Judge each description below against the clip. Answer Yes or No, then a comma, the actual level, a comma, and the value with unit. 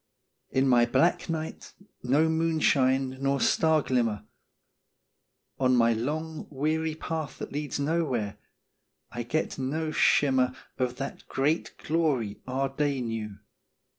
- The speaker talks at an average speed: No, slow, 120 wpm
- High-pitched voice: No, low, 135 Hz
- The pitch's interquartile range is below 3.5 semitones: No, average, 3.9 semitones